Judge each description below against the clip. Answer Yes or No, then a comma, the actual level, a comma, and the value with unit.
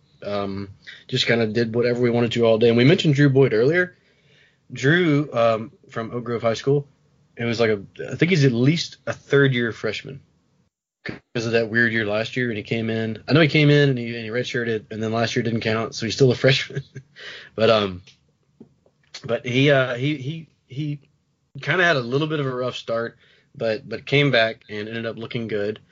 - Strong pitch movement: No, average, 3.8 semitones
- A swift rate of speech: Yes, fast, 220 wpm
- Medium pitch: No, low, 125 Hz